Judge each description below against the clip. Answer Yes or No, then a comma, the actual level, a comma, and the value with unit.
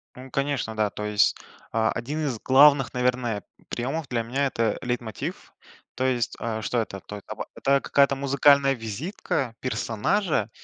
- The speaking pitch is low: Yes, low, 125 Hz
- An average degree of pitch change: Yes, average, 3.7 semitones